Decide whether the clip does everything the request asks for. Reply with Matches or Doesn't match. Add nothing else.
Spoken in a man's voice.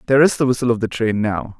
Matches